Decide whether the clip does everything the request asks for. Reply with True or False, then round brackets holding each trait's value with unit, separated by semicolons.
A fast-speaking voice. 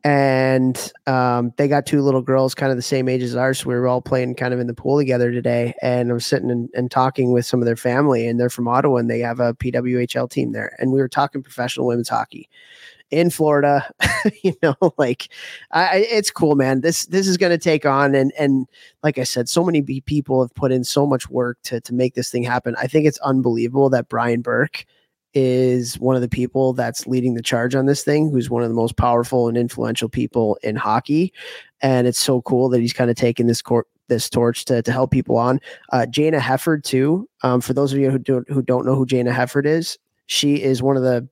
True (235 wpm)